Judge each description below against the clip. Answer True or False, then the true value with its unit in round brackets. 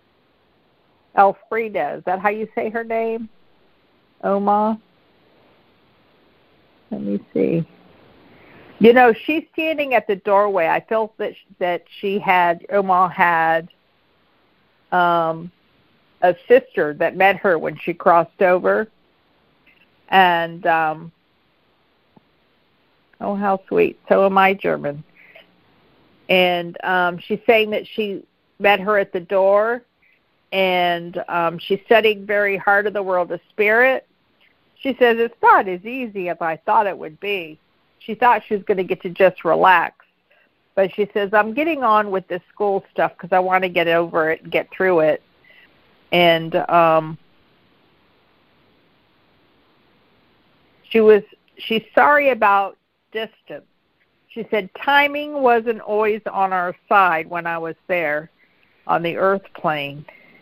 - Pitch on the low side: False (195 Hz)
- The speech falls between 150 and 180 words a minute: False (135 wpm)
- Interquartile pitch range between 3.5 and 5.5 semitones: True (4.0 semitones)